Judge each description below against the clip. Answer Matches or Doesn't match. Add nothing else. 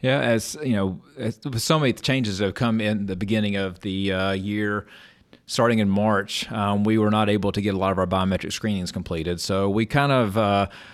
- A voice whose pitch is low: Matches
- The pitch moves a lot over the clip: Doesn't match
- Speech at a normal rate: Doesn't match